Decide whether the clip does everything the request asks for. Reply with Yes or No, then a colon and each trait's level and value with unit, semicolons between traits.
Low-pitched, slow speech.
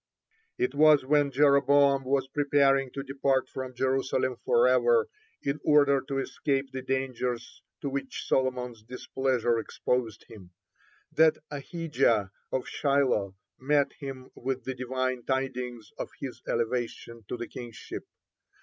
Yes: low, 130 Hz; slow, 130 wpm